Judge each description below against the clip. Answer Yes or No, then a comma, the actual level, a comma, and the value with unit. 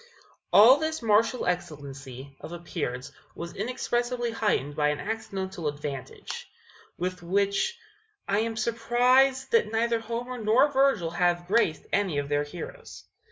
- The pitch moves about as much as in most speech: No, wide, 6.7 semitones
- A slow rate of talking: Yes, slow, 130 wpm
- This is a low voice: No, high, 200 Hz